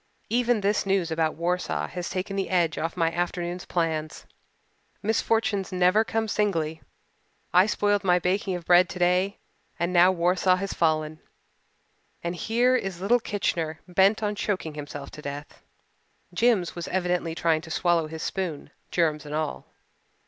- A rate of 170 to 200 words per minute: No, average, 150 wpm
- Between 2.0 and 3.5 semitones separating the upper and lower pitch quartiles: Yes, average, 3.2 semitones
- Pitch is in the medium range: Yes, medium, 180 Hz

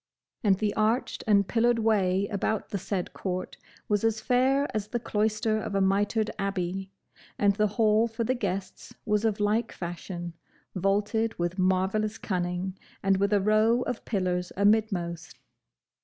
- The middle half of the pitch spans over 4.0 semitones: No, narrow, 2.5 semitones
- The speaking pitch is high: Yes, high, 205 Hz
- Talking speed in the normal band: Yes, average, 155 wpm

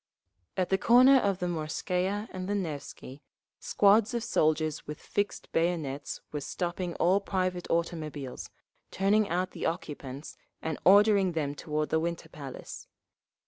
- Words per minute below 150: Yes, average, 140 wpm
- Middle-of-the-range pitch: Yes, medium, 175 Hz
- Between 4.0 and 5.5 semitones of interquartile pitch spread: Yes, average, 4.4 semitones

